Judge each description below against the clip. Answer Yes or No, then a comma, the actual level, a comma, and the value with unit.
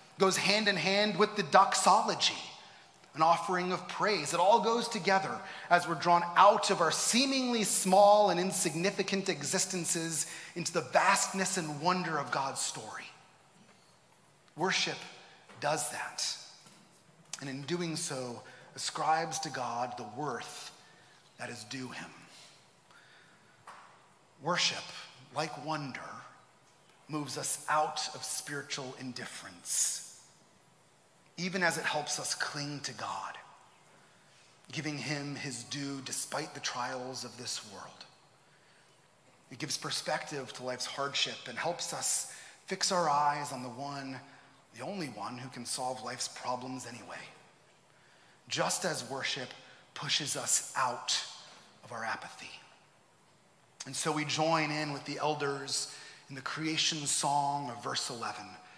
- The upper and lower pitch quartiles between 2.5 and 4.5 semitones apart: No, average, 5.1 semitones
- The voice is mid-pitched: Yes, medium, 155 Hz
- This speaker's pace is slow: Yes, slow, 130 wpm